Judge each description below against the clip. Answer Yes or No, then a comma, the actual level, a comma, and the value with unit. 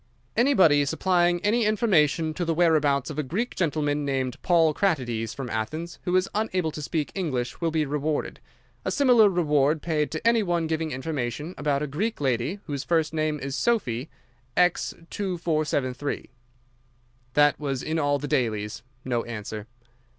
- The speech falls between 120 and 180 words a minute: Yes, average, 160 wpm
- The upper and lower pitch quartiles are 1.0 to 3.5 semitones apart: No, average, 4.0 semitones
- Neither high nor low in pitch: Yes, medium, 155 Hz